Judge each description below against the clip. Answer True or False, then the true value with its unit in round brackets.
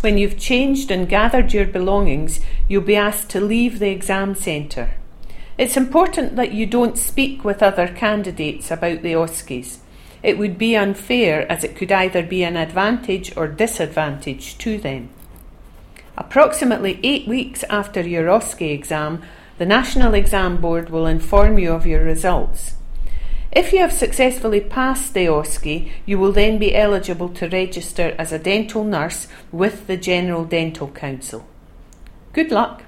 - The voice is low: False (190 Hz)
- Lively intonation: False (4.9 semitones)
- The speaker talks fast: False (155 wpm)